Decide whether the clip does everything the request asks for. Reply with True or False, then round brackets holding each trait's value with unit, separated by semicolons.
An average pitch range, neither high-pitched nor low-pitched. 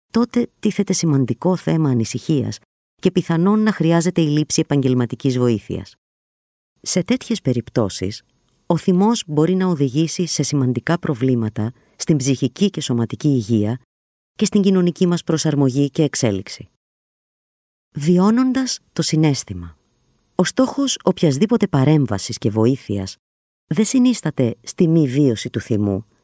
False (7.4 semitones; 145 Hz)